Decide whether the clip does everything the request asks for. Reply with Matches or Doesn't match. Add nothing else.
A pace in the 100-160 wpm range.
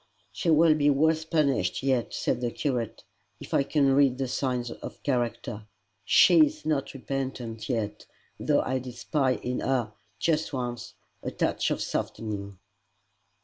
Matches